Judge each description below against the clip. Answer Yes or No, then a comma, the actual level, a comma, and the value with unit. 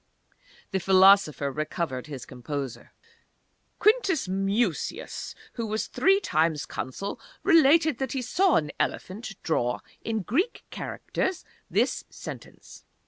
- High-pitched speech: Yes, high, 195 Hz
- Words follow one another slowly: Yes, slow, 110 wpm